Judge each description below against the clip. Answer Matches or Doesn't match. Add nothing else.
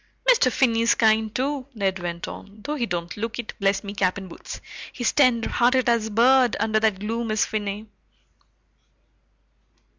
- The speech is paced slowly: Doesn't match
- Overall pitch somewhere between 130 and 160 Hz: Doesn't match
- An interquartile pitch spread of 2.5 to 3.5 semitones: Matches